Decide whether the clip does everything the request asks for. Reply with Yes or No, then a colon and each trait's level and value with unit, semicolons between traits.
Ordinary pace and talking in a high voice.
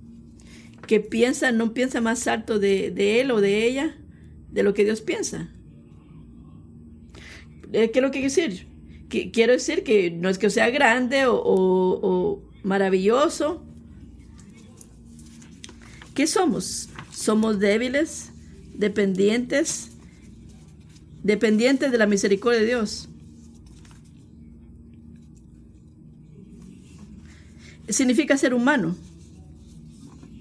No: slow, 95 wpm; high, 200 Hz